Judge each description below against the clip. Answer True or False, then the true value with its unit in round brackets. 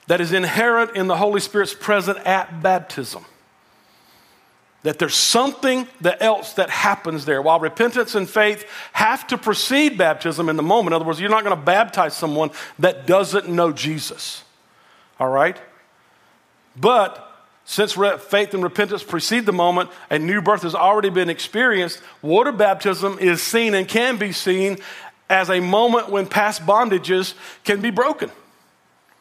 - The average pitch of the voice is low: False (195 Hz)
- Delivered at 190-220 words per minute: False (155 wpm)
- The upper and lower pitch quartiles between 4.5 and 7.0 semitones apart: False (3.2 semitones)